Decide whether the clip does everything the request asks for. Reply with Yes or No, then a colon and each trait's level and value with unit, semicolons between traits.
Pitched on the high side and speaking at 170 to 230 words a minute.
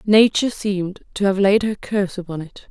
Yes: high, 195 Hz; average, 200 wpm